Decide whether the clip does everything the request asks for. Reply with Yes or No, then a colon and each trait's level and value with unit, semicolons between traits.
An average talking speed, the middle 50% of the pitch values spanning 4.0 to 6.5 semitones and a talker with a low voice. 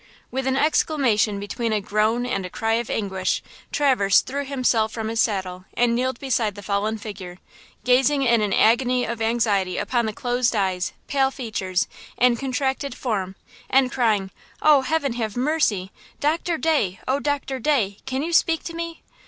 No: average, 170 wpm; average, 4.5 semitones; high, 235 Hz